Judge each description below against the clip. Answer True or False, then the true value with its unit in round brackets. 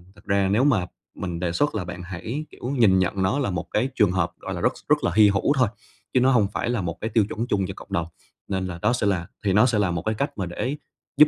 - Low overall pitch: True (100 Hz)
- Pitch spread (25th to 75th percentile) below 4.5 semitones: False (5.0 semitones)